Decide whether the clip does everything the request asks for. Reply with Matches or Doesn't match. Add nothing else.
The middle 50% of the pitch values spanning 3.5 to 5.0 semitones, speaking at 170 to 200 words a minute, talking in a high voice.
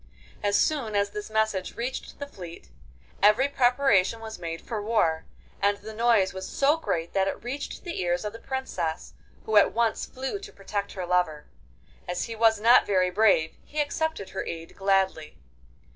Matches